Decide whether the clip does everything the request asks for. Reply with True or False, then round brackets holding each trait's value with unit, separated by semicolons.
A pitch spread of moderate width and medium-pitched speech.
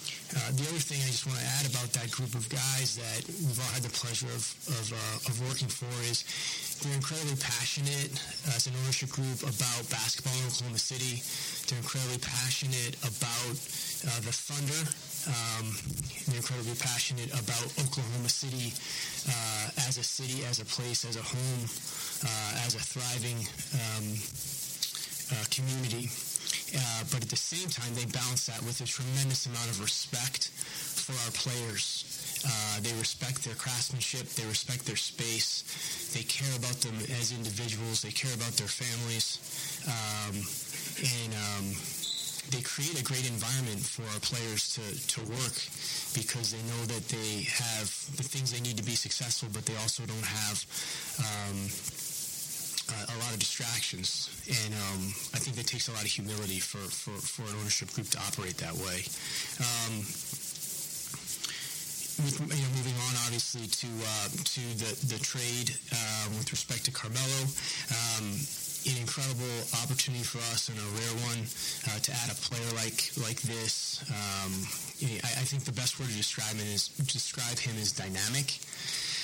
False (3.2 semitones; 125 Hz)